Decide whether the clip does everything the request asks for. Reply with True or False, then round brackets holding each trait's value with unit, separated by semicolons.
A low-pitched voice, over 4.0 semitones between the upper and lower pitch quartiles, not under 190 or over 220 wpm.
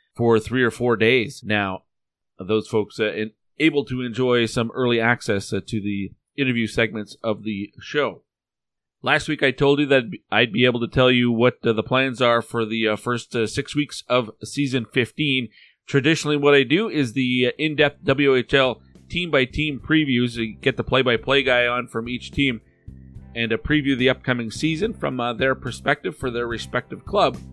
False (125 Hz; 3.3 semitones; 200 wpm)